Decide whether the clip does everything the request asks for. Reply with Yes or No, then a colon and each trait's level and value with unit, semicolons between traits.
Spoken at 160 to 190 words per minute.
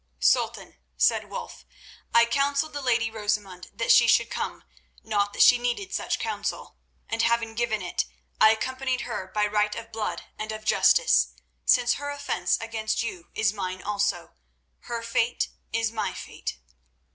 No: average, 150 wpm